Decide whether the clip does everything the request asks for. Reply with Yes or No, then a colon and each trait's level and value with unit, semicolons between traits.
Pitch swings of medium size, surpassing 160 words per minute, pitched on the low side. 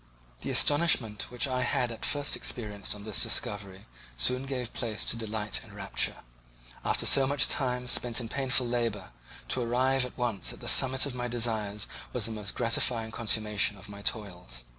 Yes: average, 3.3 semitones; average, 180 wpm; low, 115 Hz